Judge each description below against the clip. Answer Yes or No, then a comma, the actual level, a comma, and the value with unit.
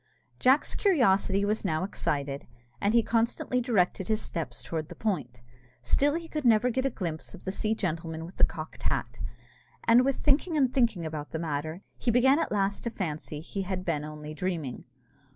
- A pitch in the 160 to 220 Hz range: Yes, high, 190 Hz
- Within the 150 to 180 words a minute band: No, average, 190 wpm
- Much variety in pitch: Yes, wide, 7.1 semitones